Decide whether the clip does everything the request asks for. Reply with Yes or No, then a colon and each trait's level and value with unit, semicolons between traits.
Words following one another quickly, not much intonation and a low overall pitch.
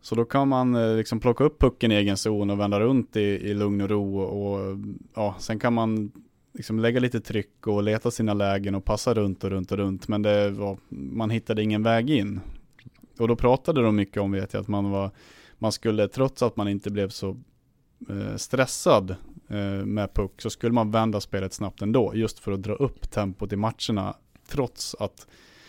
Yes: fast, 210 wpm; narrow, 2.3 semitones; low, 105 Hz